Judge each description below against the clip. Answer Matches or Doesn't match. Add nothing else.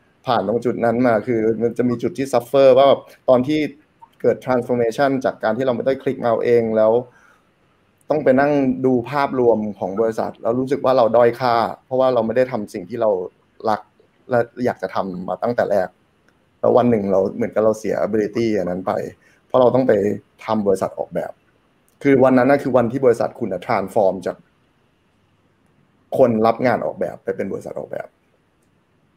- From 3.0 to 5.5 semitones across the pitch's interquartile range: Doesn't match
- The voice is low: Matches